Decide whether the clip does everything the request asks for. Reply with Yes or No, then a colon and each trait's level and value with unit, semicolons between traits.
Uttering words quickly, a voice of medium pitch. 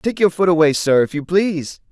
Yes: fast, 250 wpm; medium, 165 Hz